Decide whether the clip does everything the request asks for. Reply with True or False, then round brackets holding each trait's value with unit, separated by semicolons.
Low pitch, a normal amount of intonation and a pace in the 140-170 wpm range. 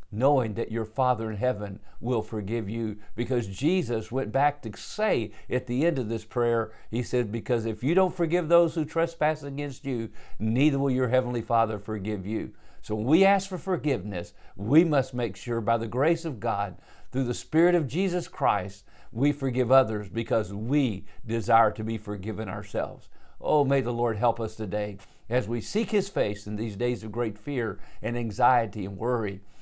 False (120 Hz; 4.0 semitones; 190 wpm)